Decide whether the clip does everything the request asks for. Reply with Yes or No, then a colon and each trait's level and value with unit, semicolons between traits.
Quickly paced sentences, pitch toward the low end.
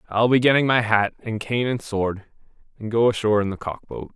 Yes: fast, 230 wpm; low, 110 Hz